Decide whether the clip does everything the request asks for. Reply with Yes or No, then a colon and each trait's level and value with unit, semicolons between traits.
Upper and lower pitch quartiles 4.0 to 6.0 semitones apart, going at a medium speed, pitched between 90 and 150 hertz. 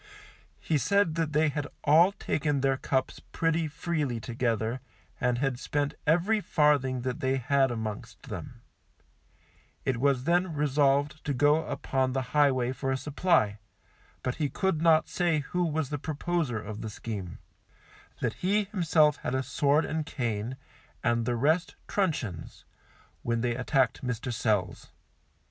Yes: average, 4.3 semitones; average, 150 wpm; medium, 140 Hz